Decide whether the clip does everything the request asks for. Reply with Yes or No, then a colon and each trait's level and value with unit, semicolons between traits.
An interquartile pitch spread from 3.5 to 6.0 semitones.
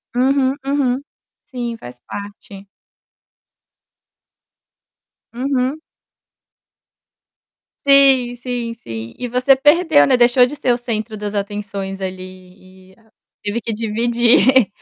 Yes: average, 4.4 semitones